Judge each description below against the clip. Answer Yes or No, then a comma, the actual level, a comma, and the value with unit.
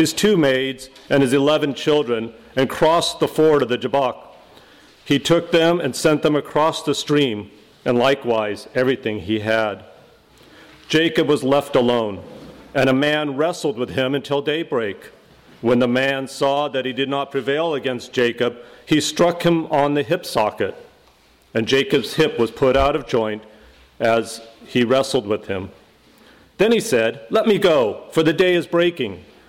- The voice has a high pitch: No, low, 135 Hz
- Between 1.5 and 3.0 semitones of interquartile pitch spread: No, average, 4.3 semitones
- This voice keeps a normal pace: Yes, average, 165 wpm